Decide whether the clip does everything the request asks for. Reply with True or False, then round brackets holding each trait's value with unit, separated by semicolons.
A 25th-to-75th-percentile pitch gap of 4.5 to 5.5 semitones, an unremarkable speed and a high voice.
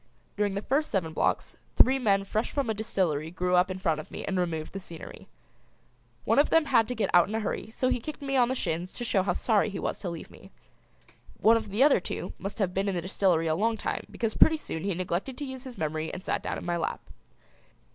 False (5.1 semitones; 255 wpm; 195 Hz)